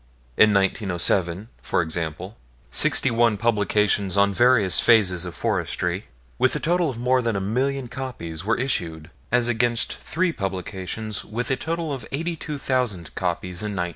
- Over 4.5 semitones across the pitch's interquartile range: Yes, average, 5.3 semitones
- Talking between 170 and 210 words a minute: No, average, 160 wpm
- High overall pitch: No, low, 105 Hz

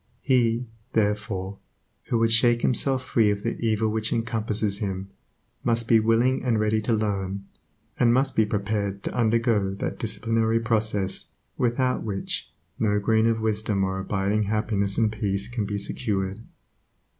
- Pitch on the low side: Yes, low, 110 Hz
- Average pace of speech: Yes, average, 150 wpm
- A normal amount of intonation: No, narrow, 2.2 semitones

